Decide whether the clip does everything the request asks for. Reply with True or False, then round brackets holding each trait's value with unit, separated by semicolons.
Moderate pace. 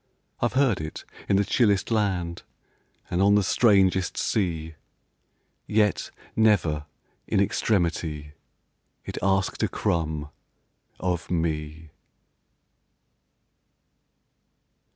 False (90 wpm)